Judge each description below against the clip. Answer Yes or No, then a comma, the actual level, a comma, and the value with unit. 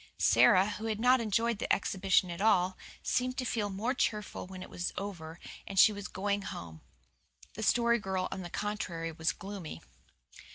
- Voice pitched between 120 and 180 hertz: No, high, 200 Hz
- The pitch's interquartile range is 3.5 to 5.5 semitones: No, average, 3.0 semitones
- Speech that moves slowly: No, average, 175 wpm